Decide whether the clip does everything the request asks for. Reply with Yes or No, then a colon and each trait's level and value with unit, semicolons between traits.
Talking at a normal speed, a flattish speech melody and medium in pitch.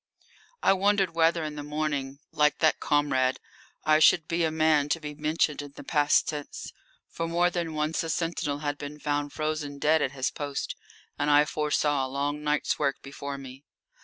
Yes: average, 190 wpm; narrow, 1.6 semitones; medium, 150 Hz